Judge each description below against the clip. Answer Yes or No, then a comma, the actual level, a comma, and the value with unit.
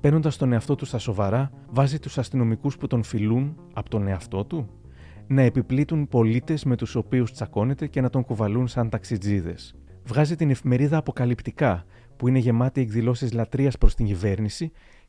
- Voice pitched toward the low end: Yes, low, 125 Hz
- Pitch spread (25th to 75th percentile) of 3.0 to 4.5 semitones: Yes, average, 3.6 semitones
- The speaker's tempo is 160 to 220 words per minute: Yes, average, 165 wpm